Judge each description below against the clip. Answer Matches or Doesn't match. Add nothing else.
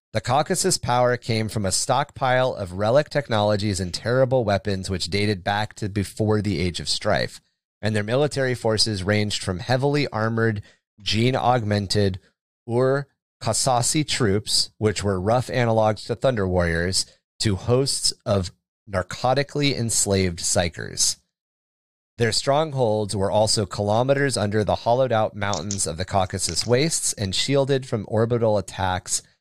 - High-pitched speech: Doesn't match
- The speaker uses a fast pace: Doesn't match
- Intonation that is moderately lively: Matches